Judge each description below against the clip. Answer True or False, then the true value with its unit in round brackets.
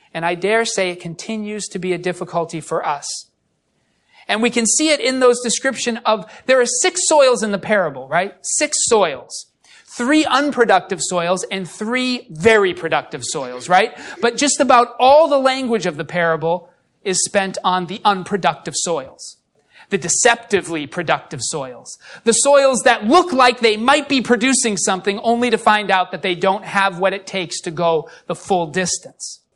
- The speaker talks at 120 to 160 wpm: False (175 wpm)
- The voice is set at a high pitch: True (205 Hz)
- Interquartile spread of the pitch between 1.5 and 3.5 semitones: False (5.6 semitones)